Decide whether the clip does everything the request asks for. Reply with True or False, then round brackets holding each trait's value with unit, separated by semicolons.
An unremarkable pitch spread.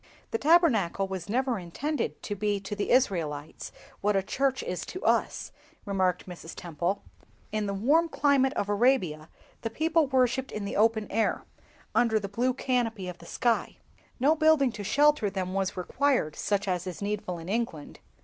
False (5.8 semitones)